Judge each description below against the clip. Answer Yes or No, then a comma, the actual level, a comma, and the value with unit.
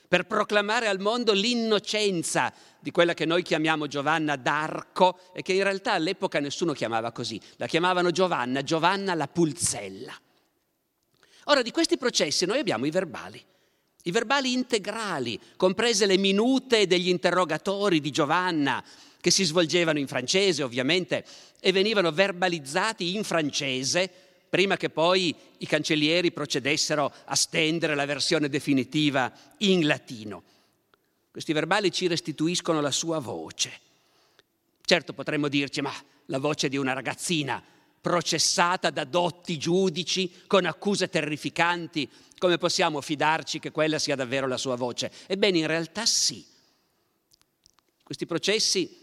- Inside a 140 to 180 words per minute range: No, average, 130 wpm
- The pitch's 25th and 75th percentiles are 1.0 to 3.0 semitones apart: No, average, 3.9 semitones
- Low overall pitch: No, medium, 170 Hz